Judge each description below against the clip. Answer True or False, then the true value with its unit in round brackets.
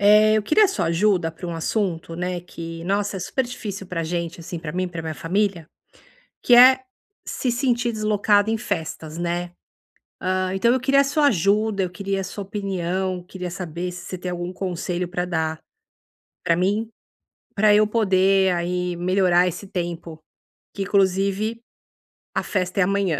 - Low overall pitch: False (185 Hz)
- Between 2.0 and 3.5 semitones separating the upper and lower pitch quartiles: True (3.0 semitones)